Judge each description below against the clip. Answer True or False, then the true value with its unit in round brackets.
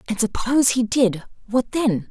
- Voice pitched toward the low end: False (230 Hz)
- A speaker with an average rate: True (170 wpm)